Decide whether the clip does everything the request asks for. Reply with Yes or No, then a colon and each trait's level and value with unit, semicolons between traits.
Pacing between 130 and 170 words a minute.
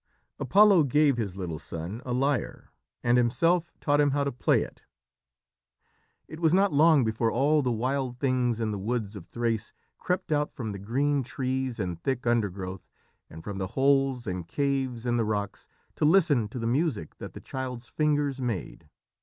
No: average, 180 wpm